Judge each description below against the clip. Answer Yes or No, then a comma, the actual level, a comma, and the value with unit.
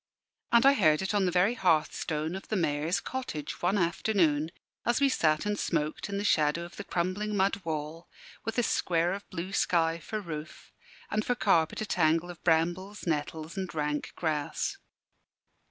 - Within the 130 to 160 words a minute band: No, average, 175 wpm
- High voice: No, medium, 175 Hz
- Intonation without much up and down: No, average, 4.3 semitones